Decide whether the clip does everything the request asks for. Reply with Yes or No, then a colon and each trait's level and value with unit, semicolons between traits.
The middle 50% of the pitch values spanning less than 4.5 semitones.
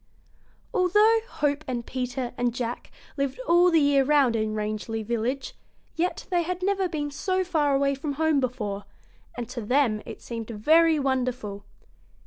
No: average, 5.3 semitones